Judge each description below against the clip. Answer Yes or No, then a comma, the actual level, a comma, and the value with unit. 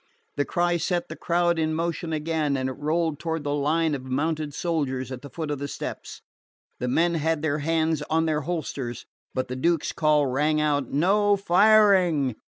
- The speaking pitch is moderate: Yes, medium, 155 Hz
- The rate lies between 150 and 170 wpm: No, average, 190 wpm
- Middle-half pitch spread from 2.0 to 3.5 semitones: Yes, average, 2.9 semitones